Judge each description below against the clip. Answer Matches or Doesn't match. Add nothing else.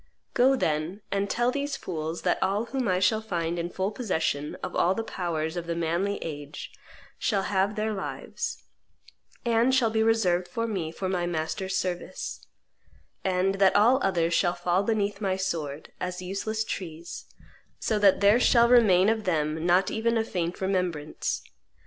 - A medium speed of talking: Matches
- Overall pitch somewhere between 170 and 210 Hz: Matches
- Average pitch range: Matches